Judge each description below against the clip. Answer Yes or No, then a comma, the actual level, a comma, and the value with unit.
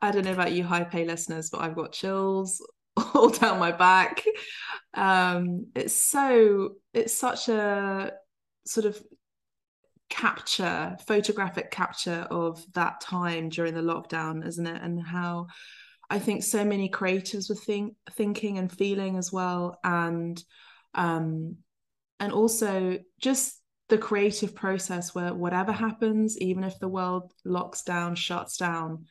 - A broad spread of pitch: No, average, 3.3 semitones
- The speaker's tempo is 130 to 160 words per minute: Yes, average, 140 wpm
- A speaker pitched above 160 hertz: Yes, medium, 185 Hz